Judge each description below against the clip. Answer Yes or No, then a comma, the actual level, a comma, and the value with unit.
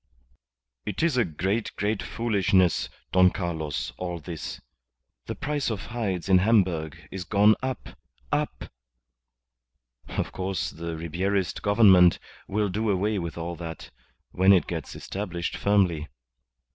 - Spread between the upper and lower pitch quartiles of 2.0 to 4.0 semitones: Yes, average, 3.4 semitones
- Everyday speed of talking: No, slow, 130 wpm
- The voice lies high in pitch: No, very low, 95 Hz